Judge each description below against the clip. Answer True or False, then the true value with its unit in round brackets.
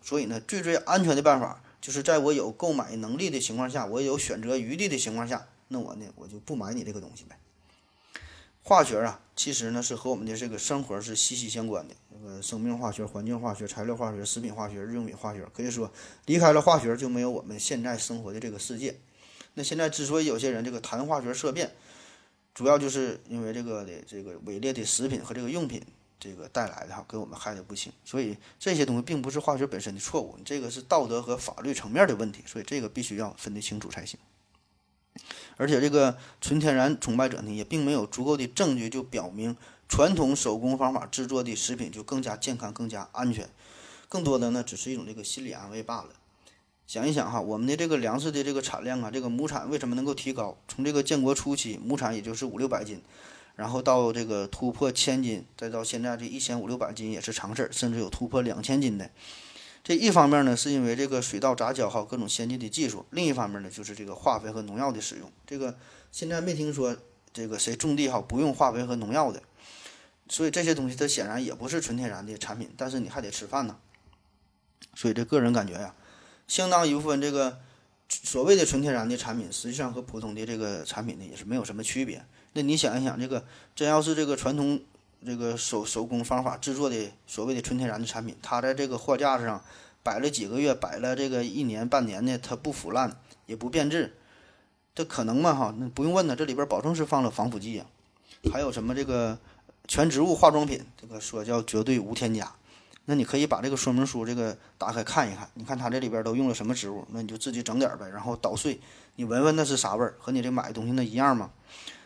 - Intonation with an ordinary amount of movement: True (3.7 semitones)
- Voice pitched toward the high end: False (120 Hz)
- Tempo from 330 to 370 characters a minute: True (345 characters per minute)